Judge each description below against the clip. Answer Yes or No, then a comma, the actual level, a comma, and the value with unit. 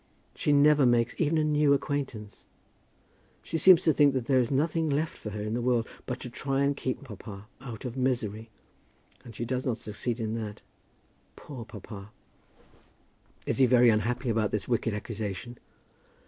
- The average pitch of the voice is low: Yes, low, 125 Hz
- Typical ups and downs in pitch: Yes, average, 4.2 semitones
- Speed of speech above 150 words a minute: Yes, average, 175 wpm